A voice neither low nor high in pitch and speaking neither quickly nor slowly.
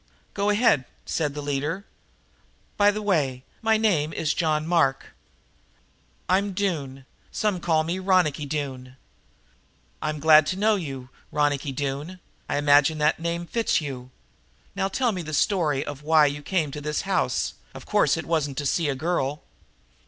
Yes: medium, 155 Hz; average, 160 wpm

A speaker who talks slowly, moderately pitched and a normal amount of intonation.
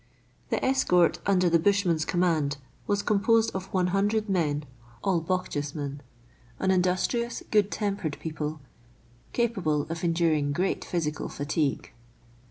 Yes: slow, 120 wpm; medium, 180 Hz; average, 4.3 semitones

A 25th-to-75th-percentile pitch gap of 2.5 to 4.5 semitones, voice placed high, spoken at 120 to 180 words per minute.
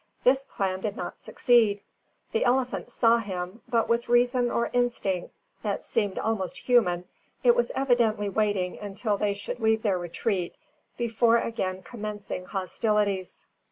Yes: average, 3.6 semitones; high, 215 Hz; average, 140 wpm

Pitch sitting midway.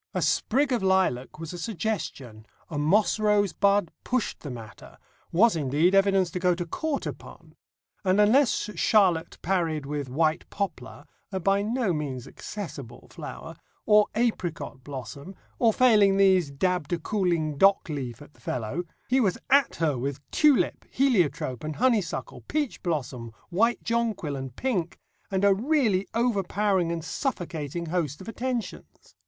Yes: medium, 180 Hz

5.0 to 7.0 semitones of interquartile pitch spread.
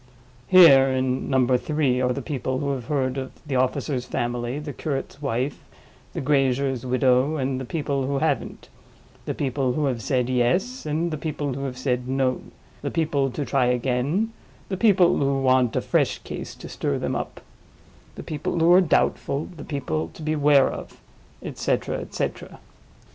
No: average, 2.7 semitones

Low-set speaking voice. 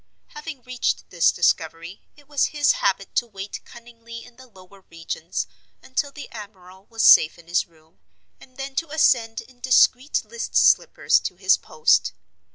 No: high, 230 Hz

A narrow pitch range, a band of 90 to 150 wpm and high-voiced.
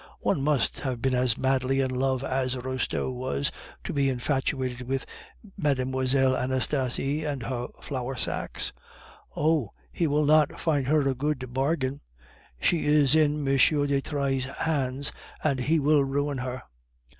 No: narrow, 2.1 semitones; average, 145 wpm; low, 135 Hz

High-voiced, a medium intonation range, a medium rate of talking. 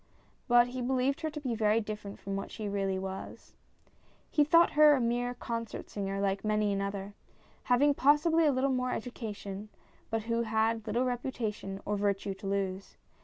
Yes: high, 225 Hz; average, 4.1 semitones; average, 170 wpm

